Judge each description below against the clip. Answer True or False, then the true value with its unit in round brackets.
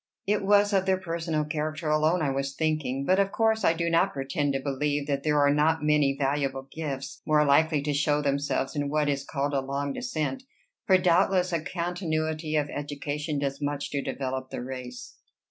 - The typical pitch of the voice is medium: True (150 Hz)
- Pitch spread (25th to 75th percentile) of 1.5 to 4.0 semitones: True (2.8 semitones)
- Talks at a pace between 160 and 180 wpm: False (195 wpm)